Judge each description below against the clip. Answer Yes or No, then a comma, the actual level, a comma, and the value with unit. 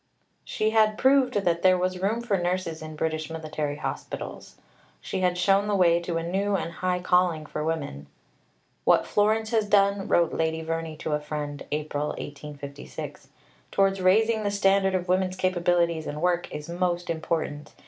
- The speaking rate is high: No, average, 170 wpm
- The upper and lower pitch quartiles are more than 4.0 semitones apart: No, average, 3.6 semitones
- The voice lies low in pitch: No, medium, 175 Hz